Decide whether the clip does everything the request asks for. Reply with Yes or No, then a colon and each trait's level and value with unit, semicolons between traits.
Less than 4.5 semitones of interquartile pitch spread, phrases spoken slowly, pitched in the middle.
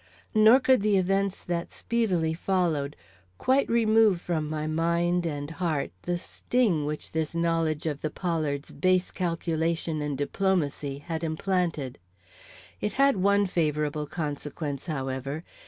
Yes: average, 3.7 semitones; slow, 130 wpm; medium, 165 Hz